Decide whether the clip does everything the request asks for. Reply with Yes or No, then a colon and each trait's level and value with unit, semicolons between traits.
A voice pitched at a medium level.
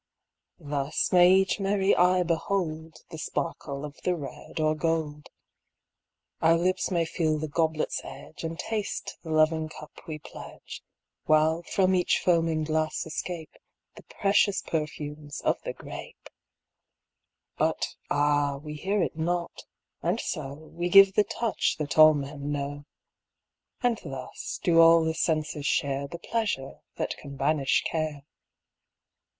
Yes: medium, 160 Hz